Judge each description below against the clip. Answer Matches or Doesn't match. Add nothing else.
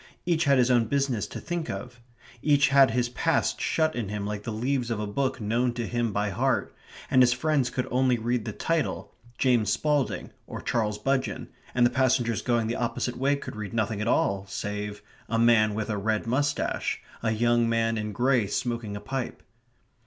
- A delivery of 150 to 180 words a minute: Doesn't match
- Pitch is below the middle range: Matches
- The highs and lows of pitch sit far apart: Doesn't match